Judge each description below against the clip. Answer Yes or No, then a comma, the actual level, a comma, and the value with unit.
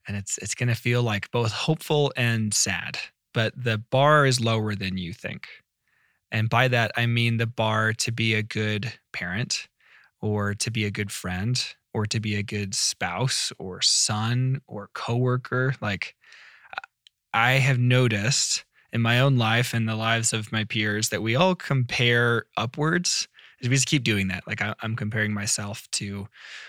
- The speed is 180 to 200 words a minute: No, average, 170 wpm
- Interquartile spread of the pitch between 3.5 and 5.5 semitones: No, average, 2.7 semitones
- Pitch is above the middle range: No, low, 115 Hz